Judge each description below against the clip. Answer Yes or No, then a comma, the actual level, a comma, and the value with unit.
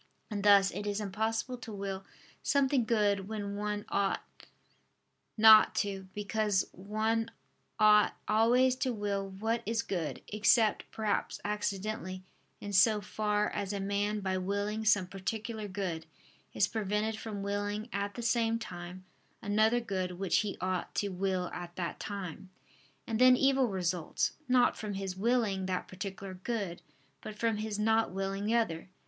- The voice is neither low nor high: No, high, 205 Hz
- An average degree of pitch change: No, narrow, 2.2 semitones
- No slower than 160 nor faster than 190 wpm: No, average, 150 wpm